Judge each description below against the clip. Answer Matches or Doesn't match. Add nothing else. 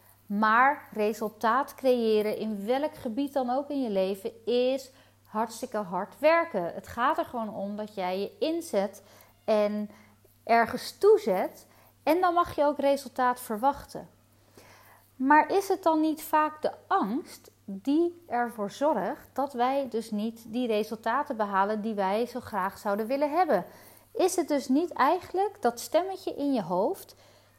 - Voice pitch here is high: Matches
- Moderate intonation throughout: Doesn't match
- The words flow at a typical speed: Matches